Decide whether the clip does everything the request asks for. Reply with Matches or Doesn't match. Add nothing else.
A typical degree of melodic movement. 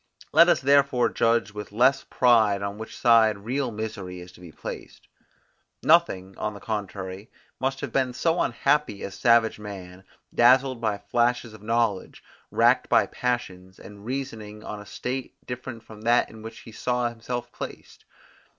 Matches